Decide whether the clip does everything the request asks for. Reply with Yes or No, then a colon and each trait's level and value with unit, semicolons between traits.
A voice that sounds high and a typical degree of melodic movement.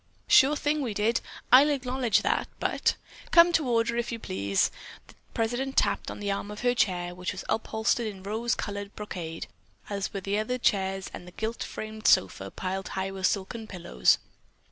Yes: high, 210 Hz; average, 3.9 semitones